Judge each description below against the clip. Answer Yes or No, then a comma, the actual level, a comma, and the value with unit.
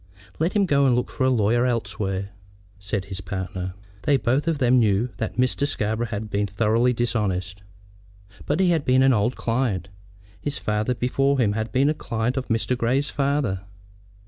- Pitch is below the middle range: Yes, low, 120 Hz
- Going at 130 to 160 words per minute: No, average, 180 wpm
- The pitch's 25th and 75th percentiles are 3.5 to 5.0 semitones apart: Yes, average, 4.5 semitones